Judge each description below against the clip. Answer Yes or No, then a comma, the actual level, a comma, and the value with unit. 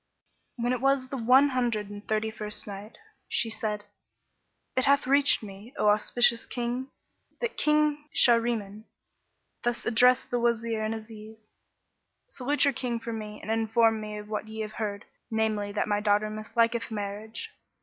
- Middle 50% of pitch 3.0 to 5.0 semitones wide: No, narrow, 2.4 semitones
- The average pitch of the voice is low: No, high, 225 Hz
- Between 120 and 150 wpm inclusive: No, average, 160 wpm